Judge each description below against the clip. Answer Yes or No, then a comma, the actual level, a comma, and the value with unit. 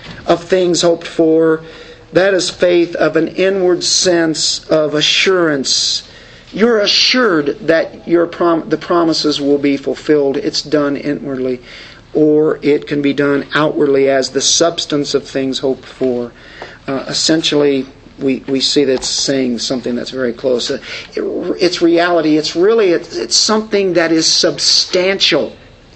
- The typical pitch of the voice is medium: Yes, medium, 155 Hz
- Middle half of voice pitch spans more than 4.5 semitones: No, average, 3.7 semitones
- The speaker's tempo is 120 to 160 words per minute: Yes, average, 155 wpm